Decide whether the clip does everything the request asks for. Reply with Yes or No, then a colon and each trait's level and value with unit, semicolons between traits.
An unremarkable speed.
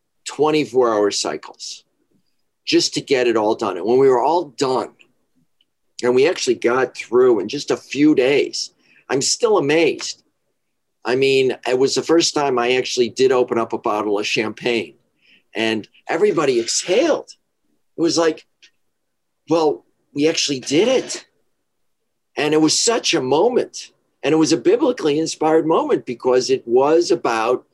Yes: average, 155 wpm